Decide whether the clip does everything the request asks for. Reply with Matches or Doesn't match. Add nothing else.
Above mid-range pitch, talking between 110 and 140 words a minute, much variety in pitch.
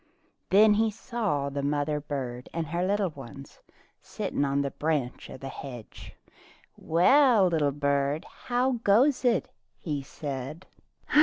Doesn't match